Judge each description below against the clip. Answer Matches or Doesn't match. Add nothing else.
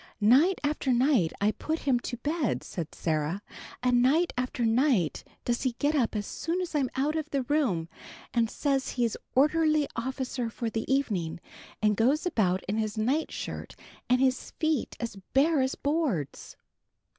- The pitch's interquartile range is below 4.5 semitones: Doesn't match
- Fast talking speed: Doesn't match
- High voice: Matches